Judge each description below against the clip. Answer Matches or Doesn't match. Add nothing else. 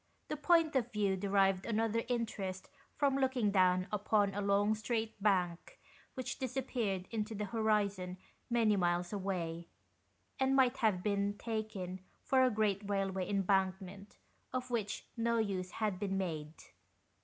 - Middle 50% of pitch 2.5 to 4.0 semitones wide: Matches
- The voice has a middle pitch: Doesn't match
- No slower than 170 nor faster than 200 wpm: Doesn't match